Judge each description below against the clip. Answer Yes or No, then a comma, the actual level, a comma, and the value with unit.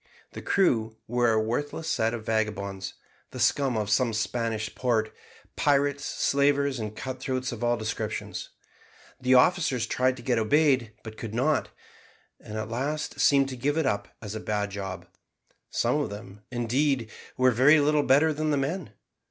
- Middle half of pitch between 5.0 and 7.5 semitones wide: No, average, 4.3 semitones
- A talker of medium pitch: No, low, 125 Hz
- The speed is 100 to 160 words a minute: No, average, 170 wpm